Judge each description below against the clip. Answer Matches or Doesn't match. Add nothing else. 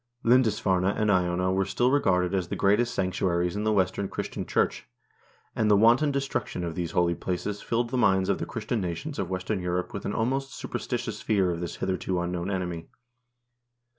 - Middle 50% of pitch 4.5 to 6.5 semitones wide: Doesn't match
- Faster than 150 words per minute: Matches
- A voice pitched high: Doesn't match